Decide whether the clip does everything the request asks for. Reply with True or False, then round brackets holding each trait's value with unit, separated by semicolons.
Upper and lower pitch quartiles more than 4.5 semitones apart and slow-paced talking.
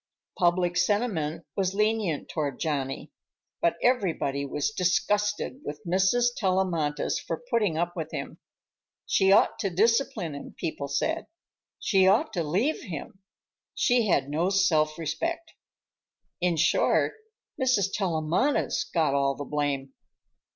True (5.3 semitones; 125 wpm)